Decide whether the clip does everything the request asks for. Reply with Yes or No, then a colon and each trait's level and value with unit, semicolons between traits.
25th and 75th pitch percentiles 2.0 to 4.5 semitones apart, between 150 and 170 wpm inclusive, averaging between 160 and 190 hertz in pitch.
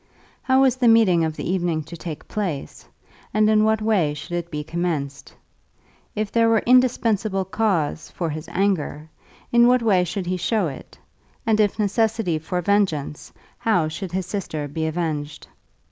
No: average, 5.3 semitones; average, 165 wpm; medium, 185 Hz